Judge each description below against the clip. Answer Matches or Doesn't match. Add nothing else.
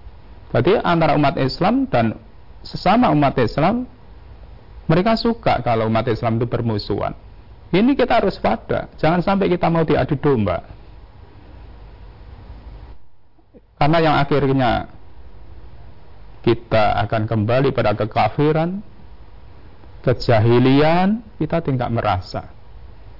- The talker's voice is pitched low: Matches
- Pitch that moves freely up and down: Matches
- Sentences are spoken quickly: Doesn't match